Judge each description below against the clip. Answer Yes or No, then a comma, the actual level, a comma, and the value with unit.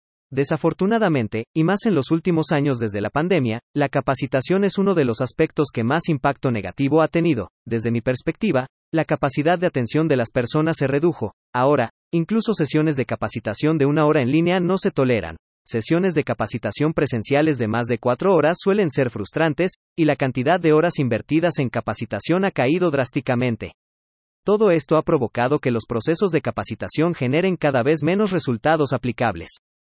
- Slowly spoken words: No, average, 175 wpm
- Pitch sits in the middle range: Yes, medium, 145 Hz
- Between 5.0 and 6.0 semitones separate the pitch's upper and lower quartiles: Yes, average, 5.3 semitones